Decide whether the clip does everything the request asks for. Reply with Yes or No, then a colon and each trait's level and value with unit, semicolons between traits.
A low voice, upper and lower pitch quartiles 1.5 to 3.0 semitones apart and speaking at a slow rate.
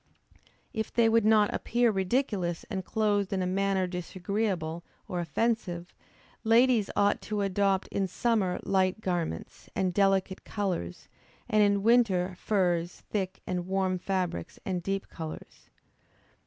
No: high, 195 Hz; average, 2.7 semitones; slow, 130 wpm